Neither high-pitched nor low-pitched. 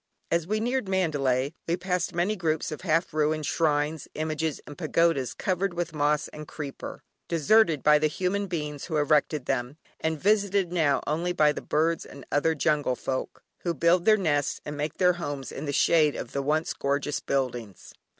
Yes: medium, 155 Hz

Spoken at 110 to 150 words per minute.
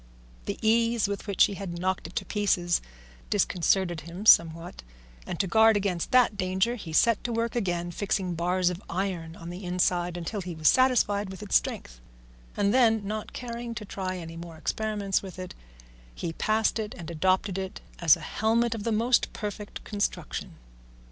No: average, 180 wpm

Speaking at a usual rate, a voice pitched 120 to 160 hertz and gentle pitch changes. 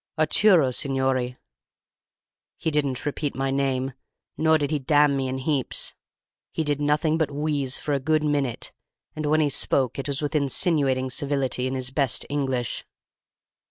Yes: average, 160 wpm; medium, 140 Hz; narrow, 2.2 semitones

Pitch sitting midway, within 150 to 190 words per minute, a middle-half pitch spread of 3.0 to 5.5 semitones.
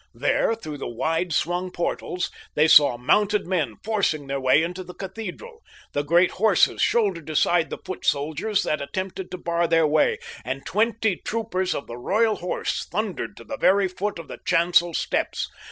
Yes: medium, 180 Hz; average, 175 wpm; average, 4.5 semitones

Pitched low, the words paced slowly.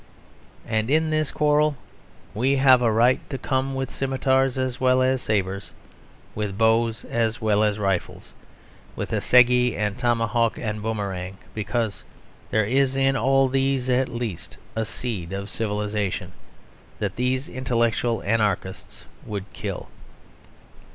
Yes: low, 115 Hz; slow, 130 wpm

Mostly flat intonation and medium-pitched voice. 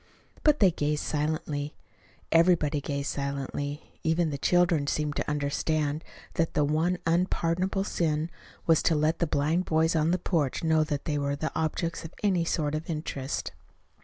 Yes: narrow, 2.3 semitones; medium, 155 Hz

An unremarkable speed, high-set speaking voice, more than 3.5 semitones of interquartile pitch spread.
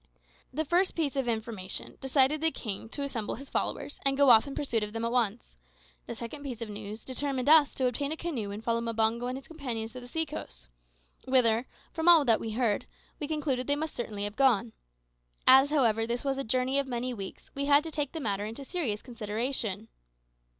No: fast, 215 wpm; very high, 250 Hz; average, 4.1 semitones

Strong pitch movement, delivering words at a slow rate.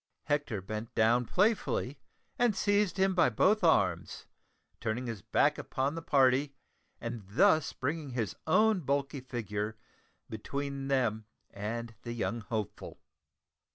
Yes: wide, 6.0 semitones; slow, 120 wpm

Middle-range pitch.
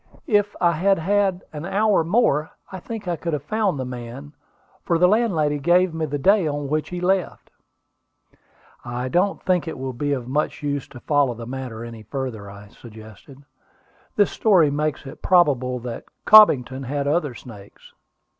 Yes: medium, 150 Hz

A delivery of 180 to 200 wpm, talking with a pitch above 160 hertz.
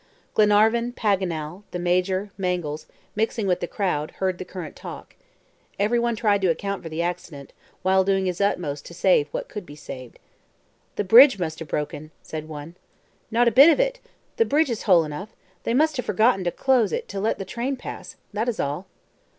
Yes: average, 190 wpm; high, 190 Hz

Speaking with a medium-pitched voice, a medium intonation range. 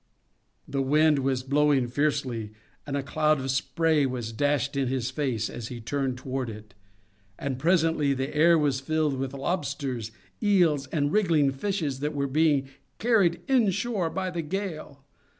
Yes: medium, 145 Hz; average, 3.3 semitones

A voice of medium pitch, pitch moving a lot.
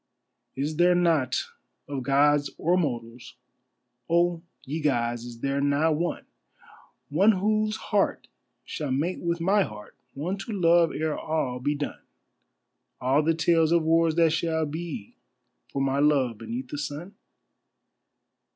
No: medium, 155 Hz; average, 3.7 semitones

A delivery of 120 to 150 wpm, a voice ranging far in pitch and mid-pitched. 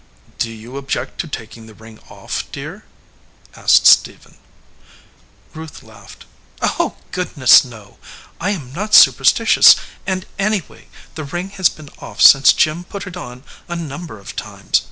Yes: average, 145 wpm; wide, 7.5 semitones; medium, 145 Hz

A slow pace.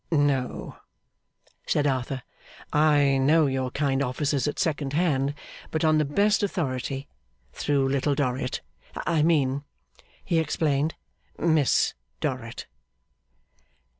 Yes: slow, 105 wpm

